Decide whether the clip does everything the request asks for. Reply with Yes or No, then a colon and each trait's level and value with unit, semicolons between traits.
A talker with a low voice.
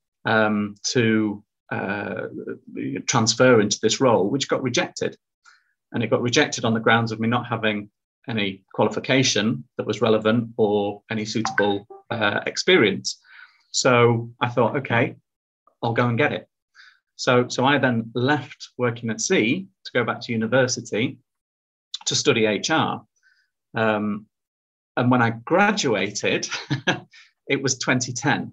Yes: low, 115 Hz